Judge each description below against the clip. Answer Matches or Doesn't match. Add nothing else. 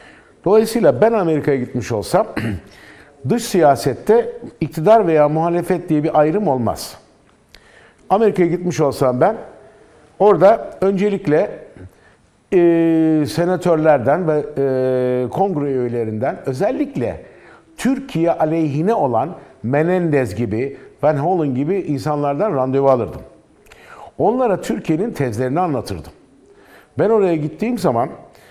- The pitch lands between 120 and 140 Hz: Doesn't match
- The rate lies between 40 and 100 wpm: Matches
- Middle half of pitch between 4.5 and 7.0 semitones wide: Matches